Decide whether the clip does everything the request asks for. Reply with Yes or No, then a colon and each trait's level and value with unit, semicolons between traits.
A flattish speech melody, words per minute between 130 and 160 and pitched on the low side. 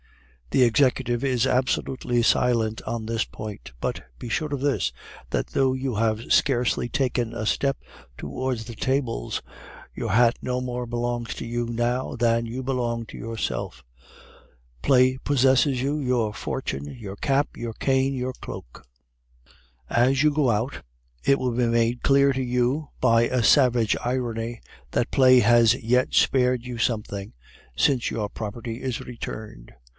Yes: narrow, 2.1 semitones; average, 150 wpm; low, 120 Hz